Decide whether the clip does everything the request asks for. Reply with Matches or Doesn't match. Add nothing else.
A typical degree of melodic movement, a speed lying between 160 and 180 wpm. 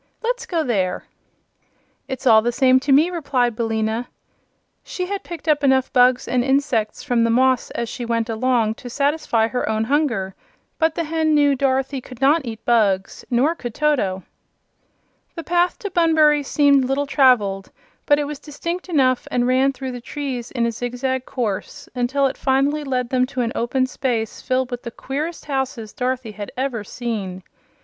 Matches